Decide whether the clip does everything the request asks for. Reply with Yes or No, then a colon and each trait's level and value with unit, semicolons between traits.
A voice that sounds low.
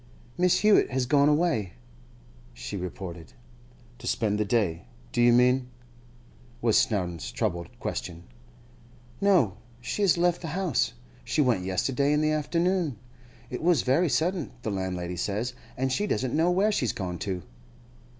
Yes: low, 125 Hz